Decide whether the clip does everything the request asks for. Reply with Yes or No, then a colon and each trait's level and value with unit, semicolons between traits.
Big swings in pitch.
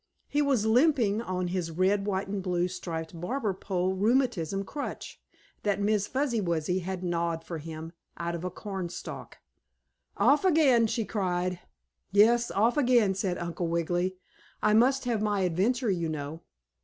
No: average, 4.6 semitones